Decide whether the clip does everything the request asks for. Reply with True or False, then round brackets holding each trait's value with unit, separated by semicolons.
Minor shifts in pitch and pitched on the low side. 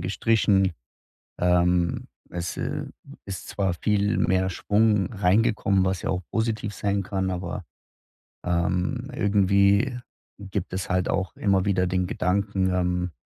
True (2.0 semitones; 95 Hz)